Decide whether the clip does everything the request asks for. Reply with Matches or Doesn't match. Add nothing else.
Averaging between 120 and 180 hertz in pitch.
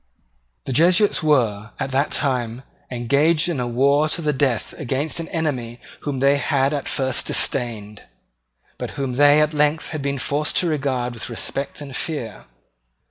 Matches